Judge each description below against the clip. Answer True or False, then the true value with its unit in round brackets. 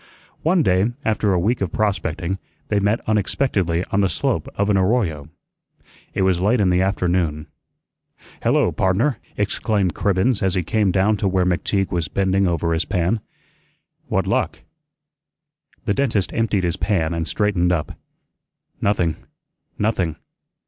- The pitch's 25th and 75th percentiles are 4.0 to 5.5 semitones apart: False (2.9 semitones)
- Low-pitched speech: True (95 Hz)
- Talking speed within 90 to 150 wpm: True (145 wpm)